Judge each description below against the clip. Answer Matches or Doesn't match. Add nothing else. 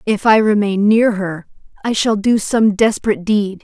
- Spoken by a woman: Matches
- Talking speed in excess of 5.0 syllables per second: Doesn't match